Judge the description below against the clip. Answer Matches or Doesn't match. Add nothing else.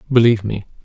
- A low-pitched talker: Matches